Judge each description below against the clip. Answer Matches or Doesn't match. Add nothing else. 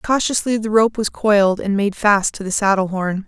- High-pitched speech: Matches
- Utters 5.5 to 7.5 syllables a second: Doesn't match